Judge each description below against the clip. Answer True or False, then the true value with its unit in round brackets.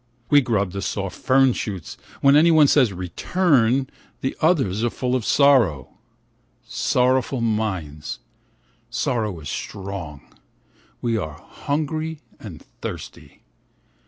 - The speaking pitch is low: True (120 Hz)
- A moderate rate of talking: False (115 wpm)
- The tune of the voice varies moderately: False (6.0 semitones)